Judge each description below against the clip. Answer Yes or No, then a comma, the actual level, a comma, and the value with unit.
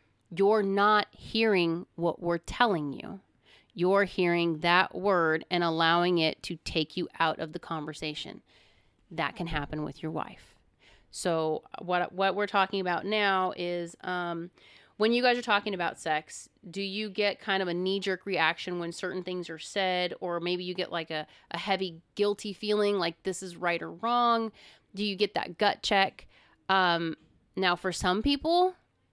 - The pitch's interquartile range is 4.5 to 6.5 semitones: No, average, 3.1 semitones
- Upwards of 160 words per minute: Yes, average, 175 wpm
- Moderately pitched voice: Yes, medium, 180 Hz